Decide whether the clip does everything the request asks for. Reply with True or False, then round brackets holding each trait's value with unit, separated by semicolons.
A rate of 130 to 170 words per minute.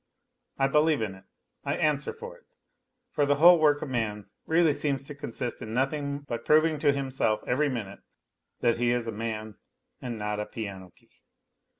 False (185 wpm)